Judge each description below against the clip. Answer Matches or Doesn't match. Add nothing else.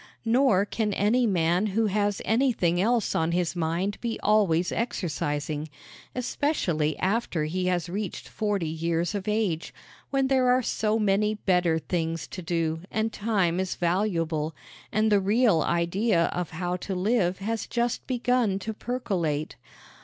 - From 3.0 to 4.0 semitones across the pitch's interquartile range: Doesn't match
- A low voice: Doesn't match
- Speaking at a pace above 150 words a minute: Doesn't match